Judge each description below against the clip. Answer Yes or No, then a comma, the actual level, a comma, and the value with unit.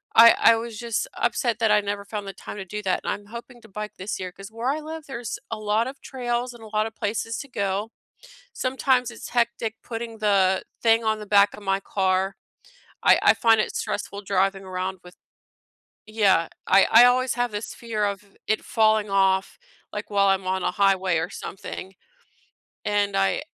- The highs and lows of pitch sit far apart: No, average, 3.0 semitones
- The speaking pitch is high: Yes, high, 210 Hz